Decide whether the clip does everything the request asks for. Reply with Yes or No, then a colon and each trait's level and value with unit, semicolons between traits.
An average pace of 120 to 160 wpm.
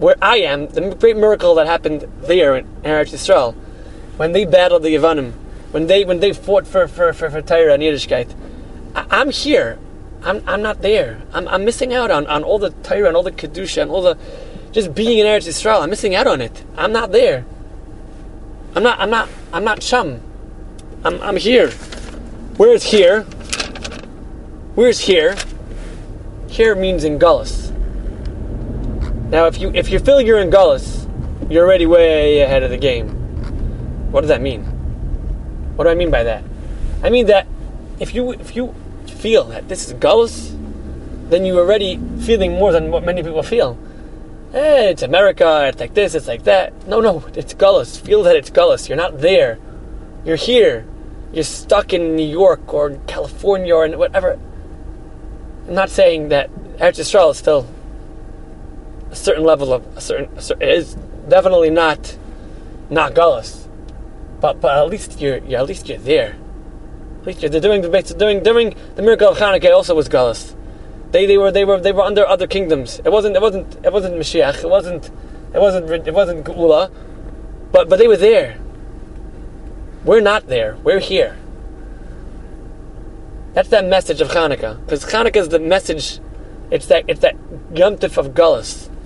No: average, 170 wpm